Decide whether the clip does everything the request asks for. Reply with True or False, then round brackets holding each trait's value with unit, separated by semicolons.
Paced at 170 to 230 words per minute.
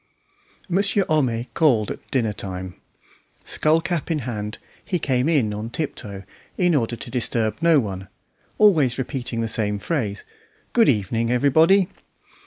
False (140 wpm)